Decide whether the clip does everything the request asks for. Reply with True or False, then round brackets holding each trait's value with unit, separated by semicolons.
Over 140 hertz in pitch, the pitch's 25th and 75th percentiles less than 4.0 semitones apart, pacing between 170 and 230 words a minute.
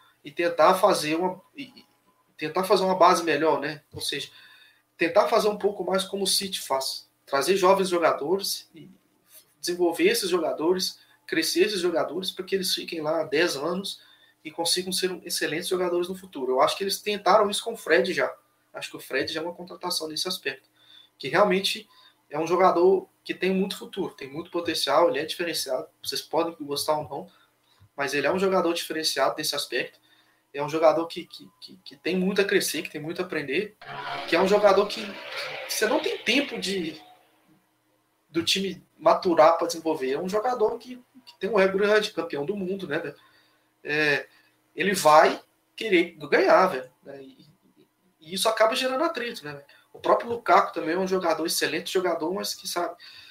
False (185 Hz; 4.4 semitones; 185 wpm)